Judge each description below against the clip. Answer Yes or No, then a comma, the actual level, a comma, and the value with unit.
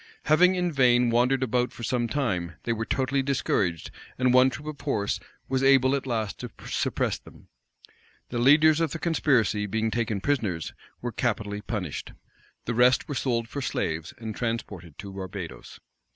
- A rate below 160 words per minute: No, average, 165 wpm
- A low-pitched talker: Yes, low, 120 Hz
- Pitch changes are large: No, average, 4.2 semitones